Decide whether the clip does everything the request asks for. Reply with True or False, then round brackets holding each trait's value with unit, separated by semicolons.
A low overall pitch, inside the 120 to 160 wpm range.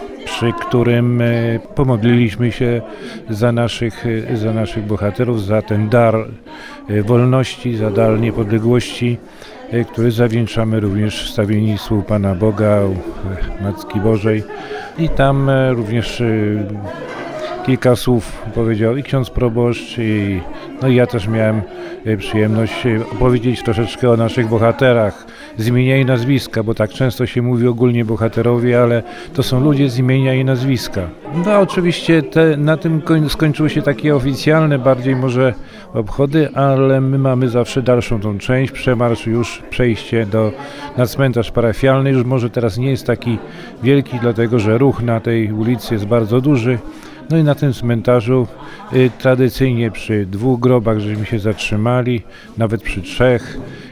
True (120 Hz; 135 wpm)